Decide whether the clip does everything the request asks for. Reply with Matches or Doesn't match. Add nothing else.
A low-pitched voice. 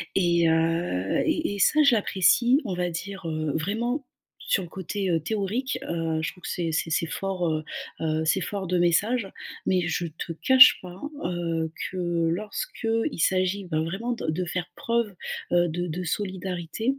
Doesn't match